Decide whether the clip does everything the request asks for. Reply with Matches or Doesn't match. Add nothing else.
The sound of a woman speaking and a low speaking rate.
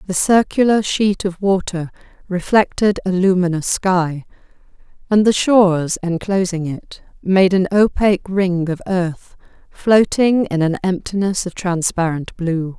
Matches